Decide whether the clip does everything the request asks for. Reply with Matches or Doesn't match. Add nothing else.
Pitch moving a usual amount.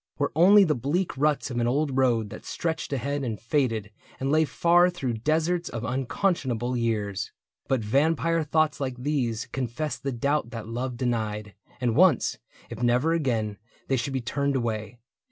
Matches